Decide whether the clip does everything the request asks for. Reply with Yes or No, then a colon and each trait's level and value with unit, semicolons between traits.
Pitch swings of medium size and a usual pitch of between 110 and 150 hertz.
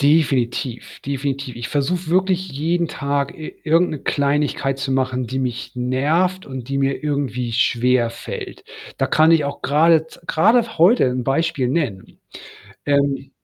Yes: average, 3.8 semitones; medium, 140 Hz